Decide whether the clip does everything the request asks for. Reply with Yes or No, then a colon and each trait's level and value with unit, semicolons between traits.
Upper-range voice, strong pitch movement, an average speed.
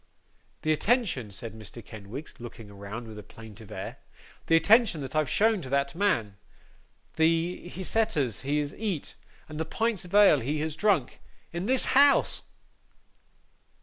No: medium, 155 Hz; wide, 8.9 semitones; average, 150 wpm